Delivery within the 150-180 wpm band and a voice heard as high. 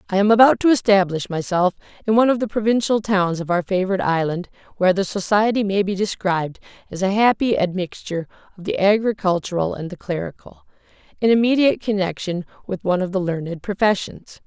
Yes: average, 170 wpm; high, 195 Hz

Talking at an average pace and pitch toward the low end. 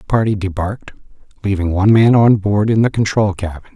Yes: average, 190 wpm; low, 100 Hz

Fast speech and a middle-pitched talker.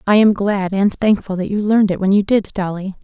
No: fast, 255 wpm; high, 200 Hz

